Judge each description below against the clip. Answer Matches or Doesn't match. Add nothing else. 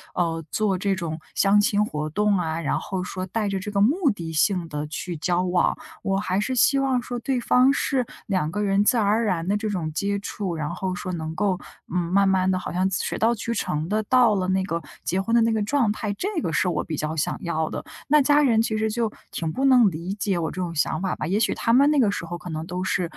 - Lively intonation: Doesn't match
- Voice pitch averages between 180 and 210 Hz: Matches